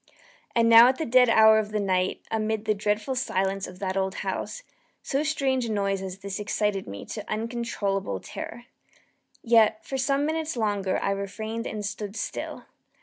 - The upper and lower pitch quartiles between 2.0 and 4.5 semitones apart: Yes, average, 3.1 semitones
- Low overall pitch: No, high, 215 Hz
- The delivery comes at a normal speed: Yes, average, 175 wpm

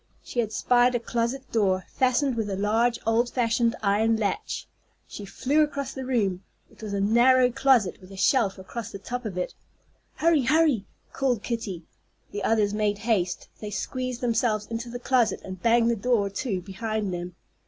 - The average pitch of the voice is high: Yes, high, 230 Hz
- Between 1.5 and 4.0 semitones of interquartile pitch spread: Yes, average, 3.6 semitones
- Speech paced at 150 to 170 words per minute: No, average, 180 wpm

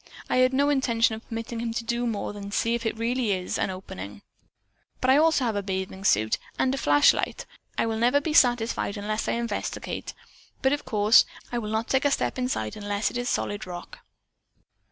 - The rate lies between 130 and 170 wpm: No, average, 200 wpm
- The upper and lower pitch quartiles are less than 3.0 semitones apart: No, average, 3.7 semitones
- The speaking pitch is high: Yes, high, 230 Hz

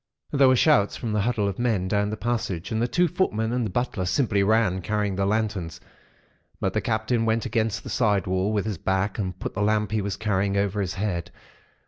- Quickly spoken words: Yes, fast, 220 wpm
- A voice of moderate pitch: No, low, 105 Hz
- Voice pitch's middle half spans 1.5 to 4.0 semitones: Yes, narrow, 2.6 semitones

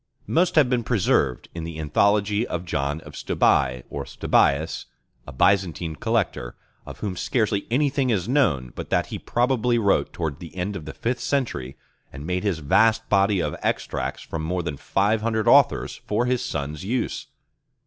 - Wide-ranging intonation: Yes, wide, 6.6 semitones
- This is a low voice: Yes, low, 100 Hz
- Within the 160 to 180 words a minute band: Yes, average, 170 wpm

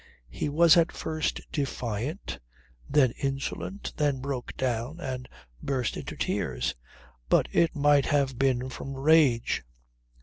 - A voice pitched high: No, low, 135 Hz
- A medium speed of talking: No, slow, 125 wpm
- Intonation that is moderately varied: Yes, average, 3.0 semitones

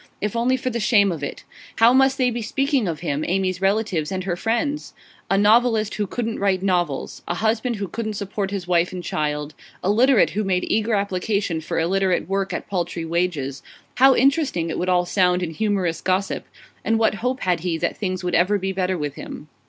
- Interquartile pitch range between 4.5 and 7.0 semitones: No, average, 3.9 semitones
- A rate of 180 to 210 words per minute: Yes, fast, 205 wpm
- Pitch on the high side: Yes, high, 195 Hz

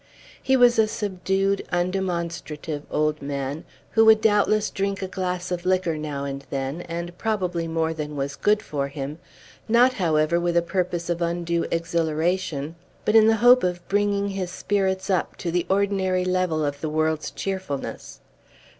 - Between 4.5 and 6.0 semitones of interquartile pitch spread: No, average, 3.7 semitones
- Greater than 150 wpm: Yes, average, 165 wpm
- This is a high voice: No, medium, 175 Hz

